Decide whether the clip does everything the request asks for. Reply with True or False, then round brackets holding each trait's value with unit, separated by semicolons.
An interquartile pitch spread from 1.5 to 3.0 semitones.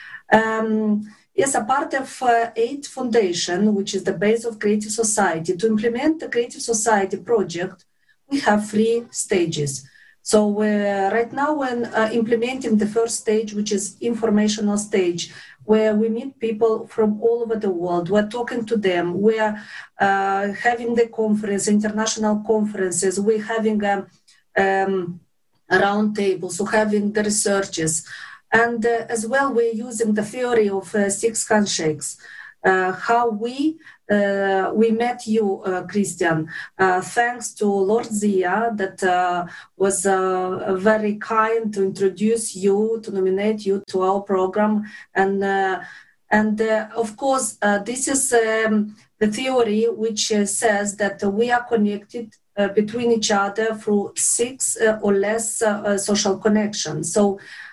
True (2.7 semitones)